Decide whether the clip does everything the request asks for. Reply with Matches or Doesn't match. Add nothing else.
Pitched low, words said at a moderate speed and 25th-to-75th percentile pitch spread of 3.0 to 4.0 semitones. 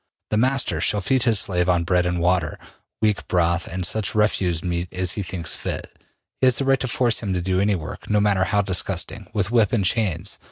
Doesn't match